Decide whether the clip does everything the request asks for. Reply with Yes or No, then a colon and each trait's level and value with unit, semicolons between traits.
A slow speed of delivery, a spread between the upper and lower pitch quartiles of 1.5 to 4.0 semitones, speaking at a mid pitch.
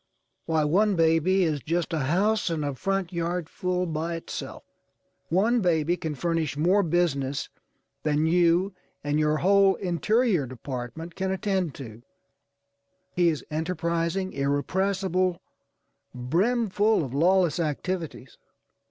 Yes: slow, 120 wpm; average, 3.7 semitones; medium, 170 Hz